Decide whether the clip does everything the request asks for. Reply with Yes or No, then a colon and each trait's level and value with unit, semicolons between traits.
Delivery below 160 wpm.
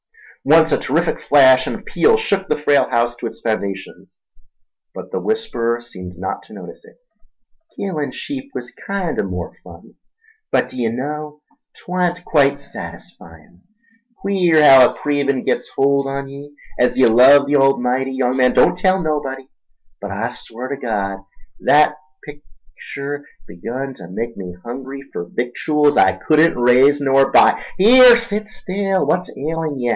Yes: average, 150 wpm